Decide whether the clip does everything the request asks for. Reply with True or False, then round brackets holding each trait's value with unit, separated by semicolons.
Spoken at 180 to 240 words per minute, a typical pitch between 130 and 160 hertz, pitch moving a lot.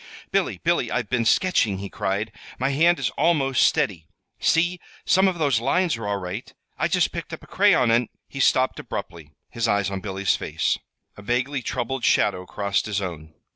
False (190 wpm; 120 Hz; 7.1 semitones)